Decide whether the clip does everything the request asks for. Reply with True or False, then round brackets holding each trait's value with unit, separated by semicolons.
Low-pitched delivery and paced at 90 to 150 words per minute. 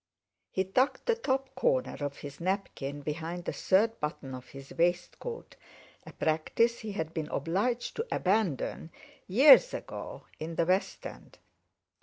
False (180 Hz; 145 wpm)